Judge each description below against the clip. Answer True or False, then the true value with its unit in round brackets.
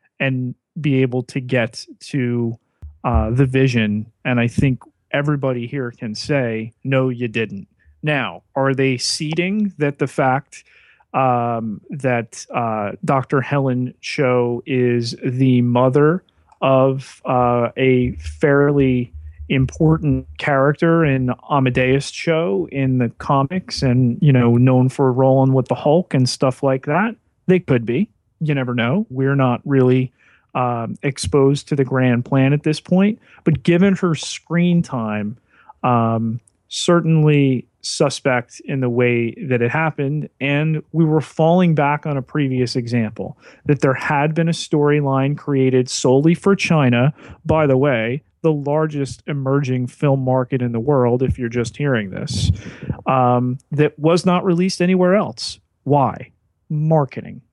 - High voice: False (135 Hz)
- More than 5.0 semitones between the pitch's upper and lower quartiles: False (3.4 semitones)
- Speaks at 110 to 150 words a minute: True (140 wpm)